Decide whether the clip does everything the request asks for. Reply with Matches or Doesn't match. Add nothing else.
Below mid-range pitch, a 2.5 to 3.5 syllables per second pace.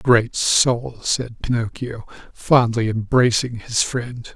Matches